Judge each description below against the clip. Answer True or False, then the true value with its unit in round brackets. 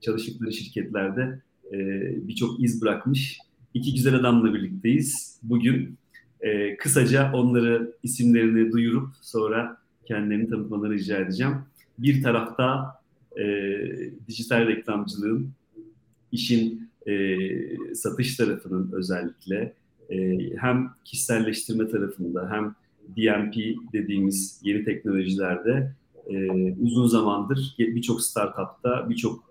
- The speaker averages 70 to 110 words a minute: True (95 wpm)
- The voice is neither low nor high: False (115 Hz)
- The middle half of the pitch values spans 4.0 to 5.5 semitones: False (3.2 semitones)